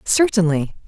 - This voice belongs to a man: No, female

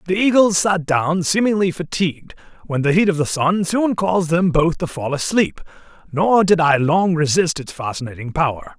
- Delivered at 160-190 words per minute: Yes, average, 185 wpm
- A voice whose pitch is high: No, medium, 170 Hz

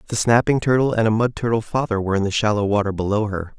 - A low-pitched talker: Yes, low, 110 Hz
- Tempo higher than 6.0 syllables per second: Yes, 6.8 syllables/s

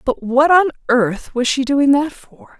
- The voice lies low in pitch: No, very high, 270 Hz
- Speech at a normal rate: No, fast, 210 wpm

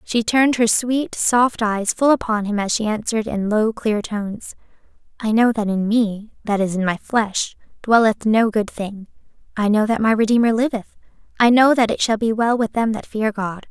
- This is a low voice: No, high, 220 Hz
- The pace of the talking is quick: Yes, fast, 210 wpm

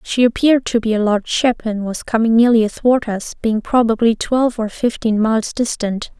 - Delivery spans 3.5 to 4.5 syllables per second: No, 5.3 syllables/s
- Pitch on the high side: Yes, high, 225 Hz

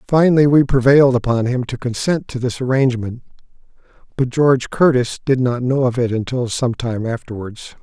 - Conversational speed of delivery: Yes, average, 170 wpm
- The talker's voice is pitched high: No, low, 125 Hz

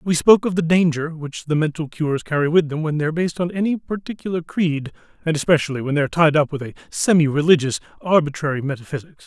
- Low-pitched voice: No, medium, 160 Hz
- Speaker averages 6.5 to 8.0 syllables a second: Yes, 6.7 syllables/s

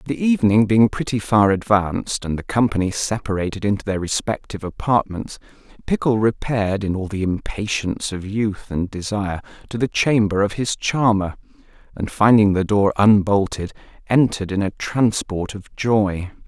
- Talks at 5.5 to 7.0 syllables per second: No, 5.1 syllables/s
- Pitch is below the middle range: Yes, low, 105 Hz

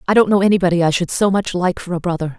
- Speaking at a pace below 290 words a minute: No, fast, 300 wpm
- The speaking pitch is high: No, medium, 180 Hz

